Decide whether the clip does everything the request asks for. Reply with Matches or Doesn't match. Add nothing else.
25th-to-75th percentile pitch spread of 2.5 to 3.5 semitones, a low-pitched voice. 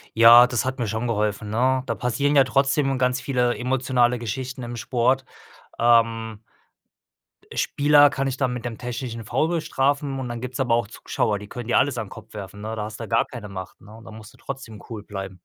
Matches